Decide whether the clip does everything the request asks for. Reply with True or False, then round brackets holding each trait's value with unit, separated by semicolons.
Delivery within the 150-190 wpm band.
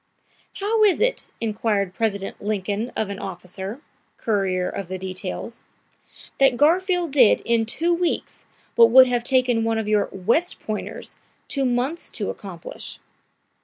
False (140 wpm)